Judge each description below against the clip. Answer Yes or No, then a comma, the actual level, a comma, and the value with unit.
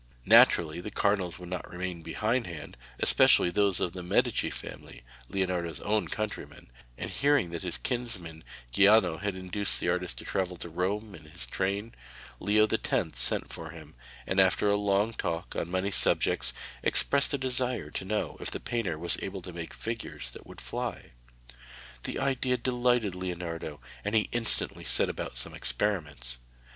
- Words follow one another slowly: No, average, 165 wpm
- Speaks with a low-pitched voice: Yes, very low, 95 Hz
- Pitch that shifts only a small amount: No, average, 4.0 semitones